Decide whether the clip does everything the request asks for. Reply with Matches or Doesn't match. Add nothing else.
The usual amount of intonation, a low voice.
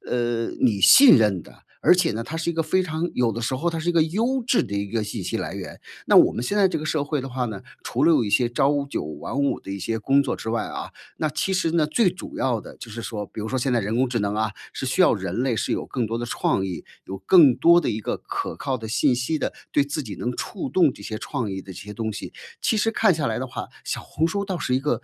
Doesn't match